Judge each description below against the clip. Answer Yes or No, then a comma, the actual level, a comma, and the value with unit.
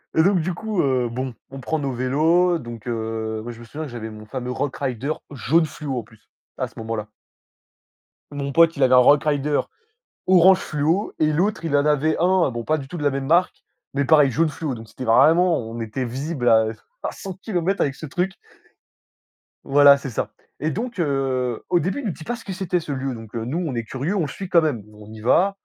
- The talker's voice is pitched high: No, medium, 140 Hz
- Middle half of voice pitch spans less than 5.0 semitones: No, wide, 5.4 semitones